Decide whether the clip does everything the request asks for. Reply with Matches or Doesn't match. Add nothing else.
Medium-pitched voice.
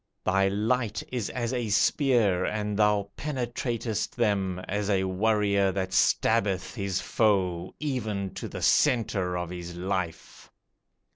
Doesn't match